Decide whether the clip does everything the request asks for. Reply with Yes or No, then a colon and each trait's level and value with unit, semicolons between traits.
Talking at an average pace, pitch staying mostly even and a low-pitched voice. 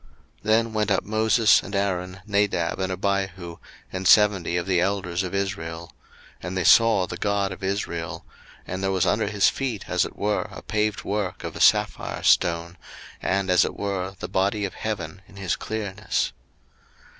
Yes: average, 180 wpm; narrow, 2.3 semitones; very low, 95 Hz